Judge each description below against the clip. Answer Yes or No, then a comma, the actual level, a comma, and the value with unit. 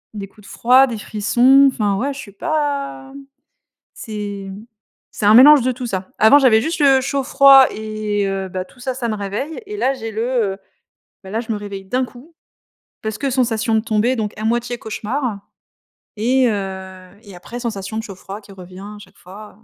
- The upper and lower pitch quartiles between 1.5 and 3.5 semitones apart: No, average, 4.3 semitones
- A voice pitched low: No, high, 220 Hz